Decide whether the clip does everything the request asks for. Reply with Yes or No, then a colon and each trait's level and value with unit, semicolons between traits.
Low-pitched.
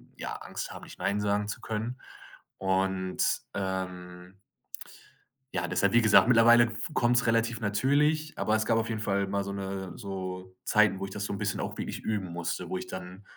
Yes: low, 100 Hz